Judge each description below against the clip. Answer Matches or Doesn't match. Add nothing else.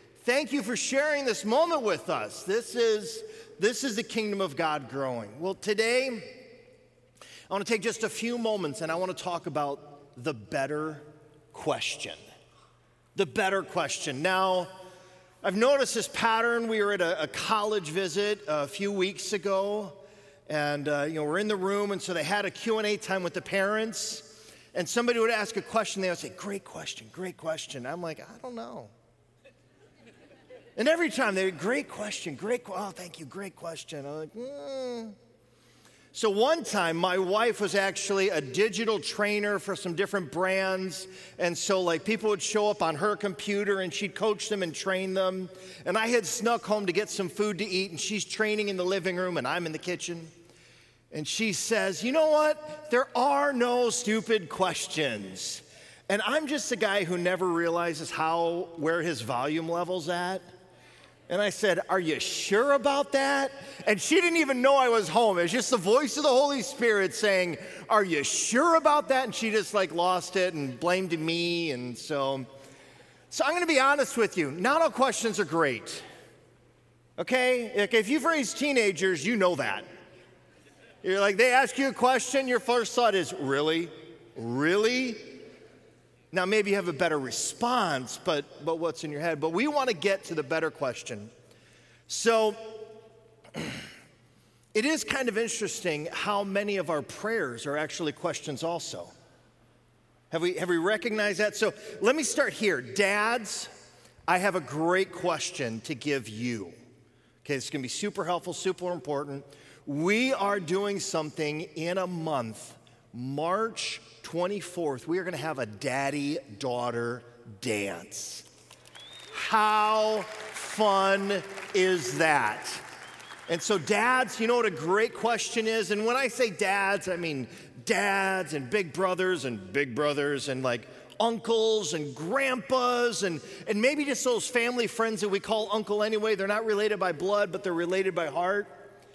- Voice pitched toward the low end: Doesn't match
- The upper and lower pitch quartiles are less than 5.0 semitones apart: Doesn't match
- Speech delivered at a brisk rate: Doesn't match